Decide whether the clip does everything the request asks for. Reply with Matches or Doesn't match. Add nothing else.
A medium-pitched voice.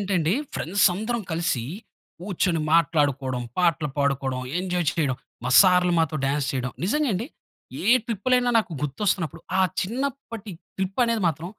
Matches